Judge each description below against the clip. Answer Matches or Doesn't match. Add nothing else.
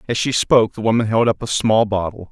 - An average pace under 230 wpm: Doesn't match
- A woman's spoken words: Doesn't match